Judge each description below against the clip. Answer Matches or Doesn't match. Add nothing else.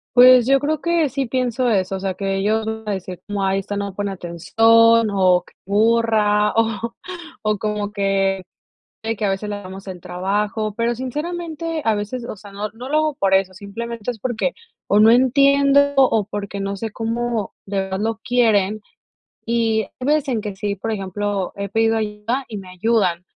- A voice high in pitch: Matches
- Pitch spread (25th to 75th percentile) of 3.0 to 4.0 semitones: Matches